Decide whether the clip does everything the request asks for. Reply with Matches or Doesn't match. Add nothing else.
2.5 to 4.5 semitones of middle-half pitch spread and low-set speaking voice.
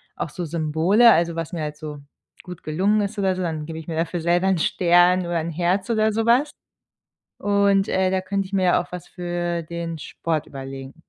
Doesn't match